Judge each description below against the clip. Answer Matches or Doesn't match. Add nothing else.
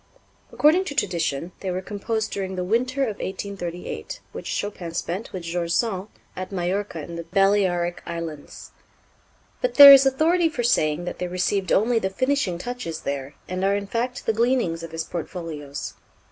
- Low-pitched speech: Doesn't match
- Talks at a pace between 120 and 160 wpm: Doesn't match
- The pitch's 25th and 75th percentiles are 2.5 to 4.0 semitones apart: Doesn't match